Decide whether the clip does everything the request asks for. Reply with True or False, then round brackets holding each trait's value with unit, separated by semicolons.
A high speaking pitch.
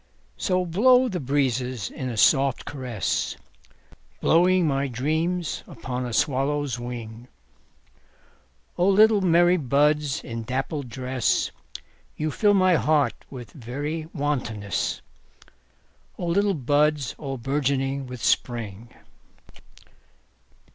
False (140 Hz)